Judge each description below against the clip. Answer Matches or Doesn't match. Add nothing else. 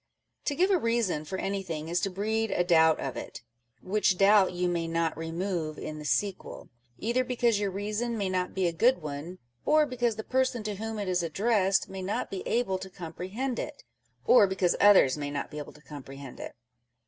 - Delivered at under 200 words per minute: Doesn't match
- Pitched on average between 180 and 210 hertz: Matches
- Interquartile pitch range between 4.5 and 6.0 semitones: Matches